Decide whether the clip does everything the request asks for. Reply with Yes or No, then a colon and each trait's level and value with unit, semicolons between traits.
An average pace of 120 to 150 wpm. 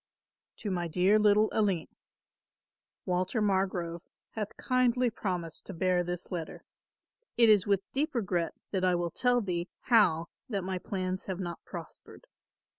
Yes: average, 145 wpm